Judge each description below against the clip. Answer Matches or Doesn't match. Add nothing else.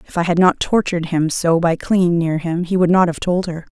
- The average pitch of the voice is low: Doesn't match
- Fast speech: Matches